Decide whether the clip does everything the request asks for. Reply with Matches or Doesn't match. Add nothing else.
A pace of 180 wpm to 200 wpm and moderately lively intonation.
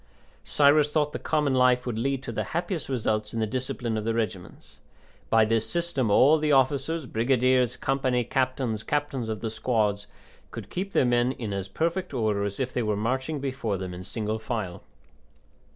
Matches